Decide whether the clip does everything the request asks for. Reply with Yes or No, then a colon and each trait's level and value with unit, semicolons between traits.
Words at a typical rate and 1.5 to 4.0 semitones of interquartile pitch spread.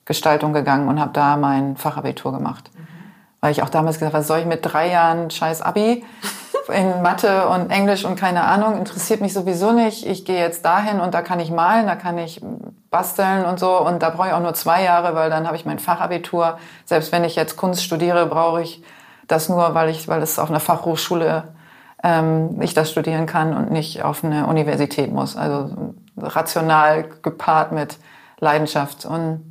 No: fast, 195 wpm; average, 2.8 semitones